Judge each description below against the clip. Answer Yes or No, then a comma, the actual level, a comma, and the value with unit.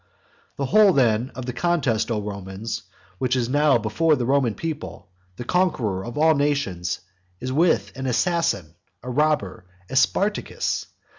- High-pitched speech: No, low, 130 Hz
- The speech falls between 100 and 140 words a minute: No, average, 150 wpm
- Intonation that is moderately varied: No, wide, 5.7 semitones